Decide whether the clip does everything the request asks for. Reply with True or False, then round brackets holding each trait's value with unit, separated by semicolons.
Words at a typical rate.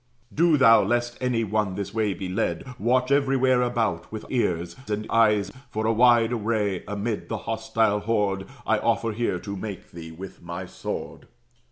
True (170 wpm)